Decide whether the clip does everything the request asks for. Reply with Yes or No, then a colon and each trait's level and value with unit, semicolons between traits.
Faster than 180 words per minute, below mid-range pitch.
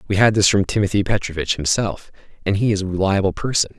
Yes: fast, 205 wpm; low, 100 Hz